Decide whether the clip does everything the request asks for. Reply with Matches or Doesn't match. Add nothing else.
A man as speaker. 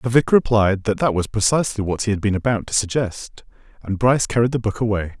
Matches